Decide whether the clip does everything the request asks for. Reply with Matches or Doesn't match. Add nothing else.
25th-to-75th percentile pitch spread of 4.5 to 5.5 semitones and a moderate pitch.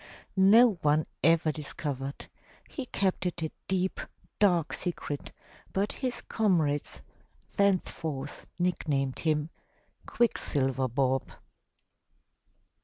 Matches